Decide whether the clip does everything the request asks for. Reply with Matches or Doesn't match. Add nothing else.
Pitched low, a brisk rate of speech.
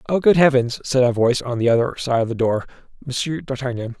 Matches